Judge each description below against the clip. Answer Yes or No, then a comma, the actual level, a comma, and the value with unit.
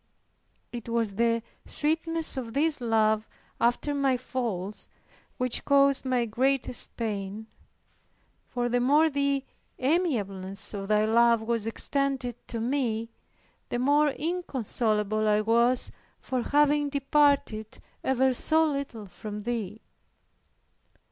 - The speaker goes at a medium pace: No, slow, 115 wpm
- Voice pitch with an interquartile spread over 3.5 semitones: Yes, average, 4.2 semitones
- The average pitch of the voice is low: No, high, 240 Hz